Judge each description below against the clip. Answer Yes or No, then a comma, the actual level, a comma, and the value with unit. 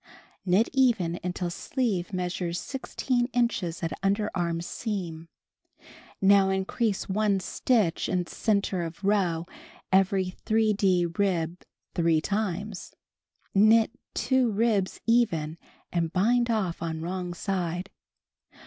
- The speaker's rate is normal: No, slow, 110 wpm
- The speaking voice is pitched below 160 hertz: No, high, 190 Hz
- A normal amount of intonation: Yes, average, 3.8 semitones